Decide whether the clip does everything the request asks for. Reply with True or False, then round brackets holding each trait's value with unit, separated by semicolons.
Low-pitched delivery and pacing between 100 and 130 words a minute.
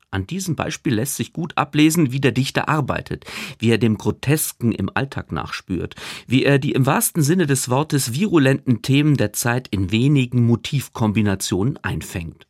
False (130 Hz; 165 wpm)